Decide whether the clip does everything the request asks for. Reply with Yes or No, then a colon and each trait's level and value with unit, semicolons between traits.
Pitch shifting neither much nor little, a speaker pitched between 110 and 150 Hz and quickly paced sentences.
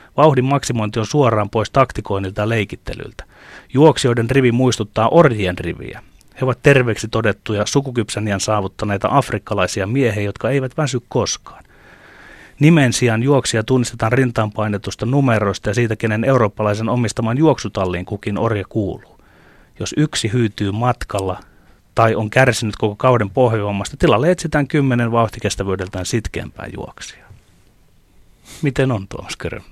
No: average, 3.8 semitones; low, 115 Hz; average, 120 wpm